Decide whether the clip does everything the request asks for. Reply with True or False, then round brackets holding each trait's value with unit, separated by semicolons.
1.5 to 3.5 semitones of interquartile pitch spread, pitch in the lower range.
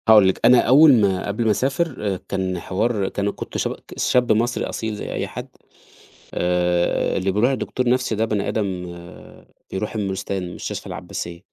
False (4.1 semitones; 105 Hz)